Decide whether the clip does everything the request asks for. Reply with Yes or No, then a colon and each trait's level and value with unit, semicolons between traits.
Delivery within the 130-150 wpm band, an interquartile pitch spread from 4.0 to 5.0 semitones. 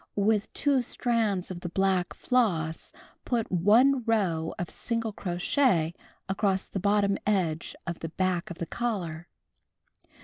Yes: slow, 135 wpm; average, 4.5 semitones